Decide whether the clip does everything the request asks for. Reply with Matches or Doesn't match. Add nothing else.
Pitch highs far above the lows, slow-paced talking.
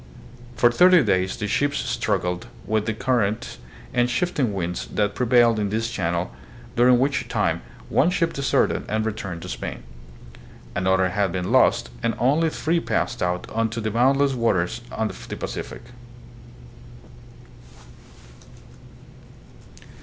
Doesn't match